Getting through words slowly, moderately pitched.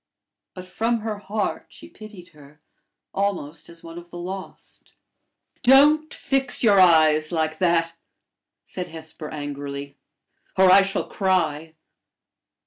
Yes: slow, 125 wpm; medium, 175 Hz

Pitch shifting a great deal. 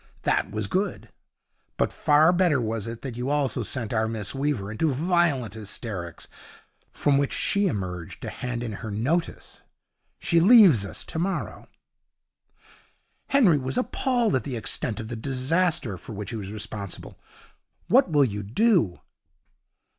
Yes: wide, 7.4 semitones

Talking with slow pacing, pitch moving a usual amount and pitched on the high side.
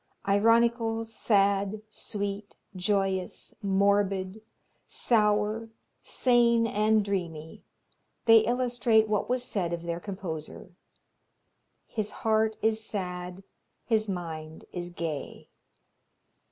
Yes: slow, 90 wpm; average, 3.1 semitones; high, 205 Hz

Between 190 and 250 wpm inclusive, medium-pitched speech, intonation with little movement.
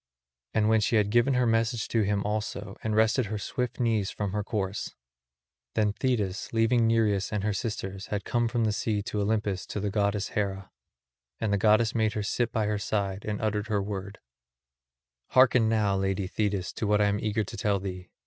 No: average, 200 wpm; low, 105 Hz; narrow, 1.8 semitones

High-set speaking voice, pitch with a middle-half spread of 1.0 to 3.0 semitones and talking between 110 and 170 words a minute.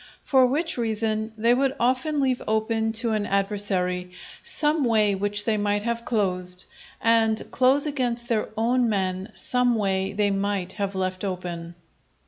No: high, 220 Hz; average, 3.7 semitones; average, 150 wpm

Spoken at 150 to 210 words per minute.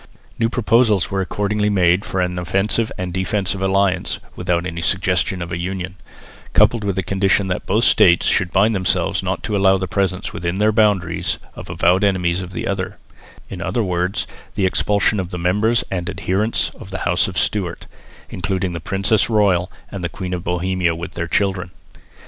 Yes: average, 185 wpm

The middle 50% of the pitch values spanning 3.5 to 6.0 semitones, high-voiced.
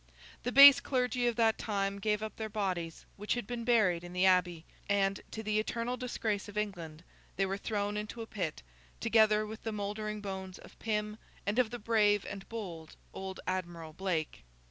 No: average, 2.7 semitones; high, 210 Hz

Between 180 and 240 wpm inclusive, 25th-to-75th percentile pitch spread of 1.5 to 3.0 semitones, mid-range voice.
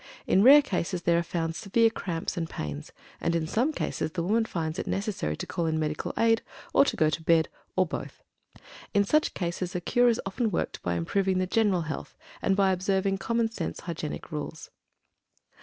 No: average, 195 wpm; average, 4.2 semitones; medium, 180 Hz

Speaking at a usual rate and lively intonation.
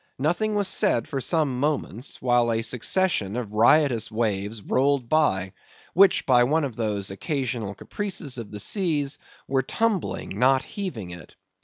Yes: average, 150 wpm; wide, 5.9 semitones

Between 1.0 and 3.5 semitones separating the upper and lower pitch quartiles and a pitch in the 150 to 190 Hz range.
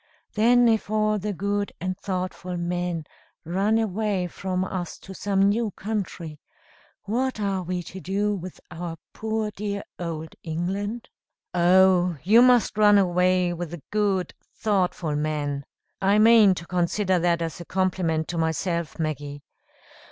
Yes: average, 3.1 semitones; medium, 185 Hz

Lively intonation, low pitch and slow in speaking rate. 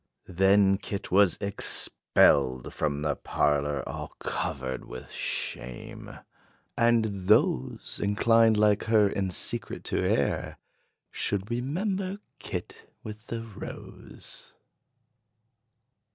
Yes: wide, 7.2 semitones; low, 100 Hz; slow, 95 wpm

